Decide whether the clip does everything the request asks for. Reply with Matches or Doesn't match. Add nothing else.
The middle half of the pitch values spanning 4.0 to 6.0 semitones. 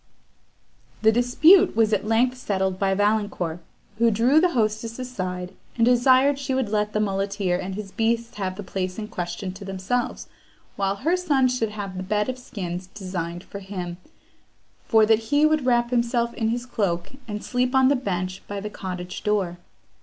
Matches